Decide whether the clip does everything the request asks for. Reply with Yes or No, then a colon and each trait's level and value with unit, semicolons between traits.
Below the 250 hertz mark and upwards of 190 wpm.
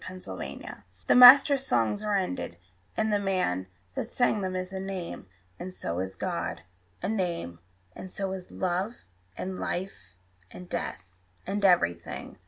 No: medium, 185 Hz; average, 155 wpm